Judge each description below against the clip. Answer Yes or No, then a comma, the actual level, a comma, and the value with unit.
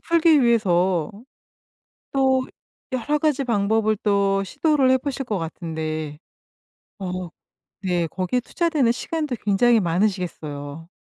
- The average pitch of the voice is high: Yes, high, 210 Hz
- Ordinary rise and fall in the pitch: No, wide, 6.7 semitones